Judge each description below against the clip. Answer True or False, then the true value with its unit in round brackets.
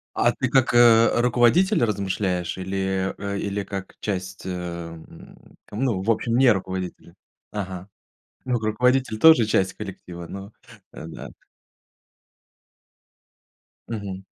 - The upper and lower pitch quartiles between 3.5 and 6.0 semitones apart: True (4.0 semitones)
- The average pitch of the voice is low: True (100 Hz)